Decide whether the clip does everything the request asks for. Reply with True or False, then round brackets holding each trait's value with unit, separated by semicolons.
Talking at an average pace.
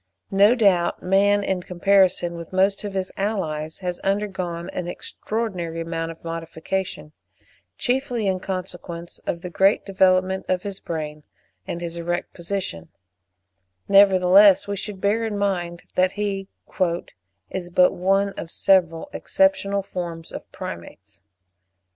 False (130 wpm)